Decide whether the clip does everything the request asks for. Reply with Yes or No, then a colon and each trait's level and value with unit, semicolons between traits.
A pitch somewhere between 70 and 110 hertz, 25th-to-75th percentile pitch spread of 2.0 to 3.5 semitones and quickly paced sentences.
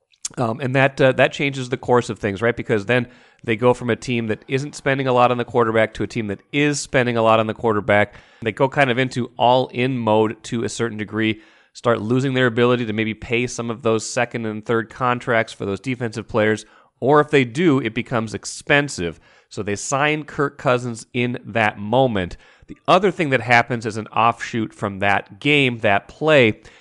No: low, 120 Hz; average, 2.9 semitones; fast, 210 wpm